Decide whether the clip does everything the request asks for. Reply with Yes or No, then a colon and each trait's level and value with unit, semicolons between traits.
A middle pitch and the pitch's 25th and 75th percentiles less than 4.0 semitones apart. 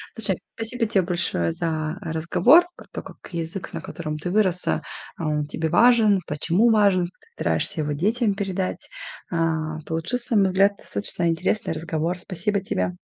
No: medium, 175 Hz; average, 4.3 semitones